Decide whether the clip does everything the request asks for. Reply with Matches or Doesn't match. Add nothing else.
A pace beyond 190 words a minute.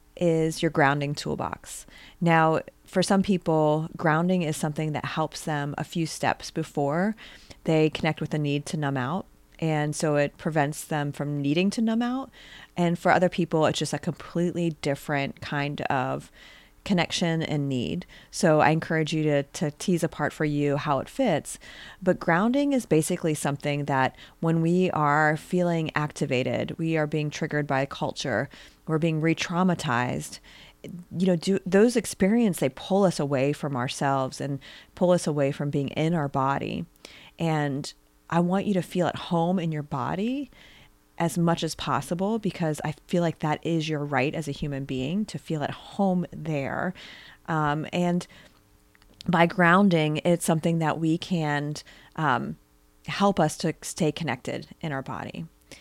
Doesn't match